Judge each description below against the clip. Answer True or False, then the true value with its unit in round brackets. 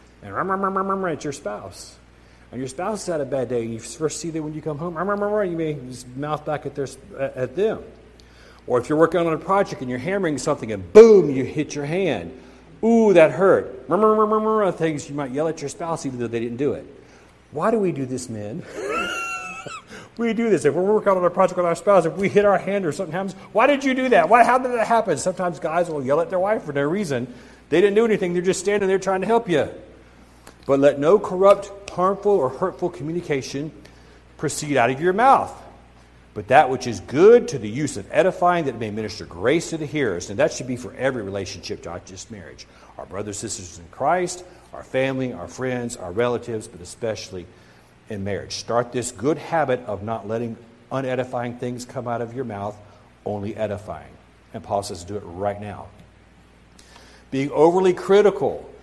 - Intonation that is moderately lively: False (8.3 semitones)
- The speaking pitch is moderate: True (145 Hz)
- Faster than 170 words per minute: True (205 wpm)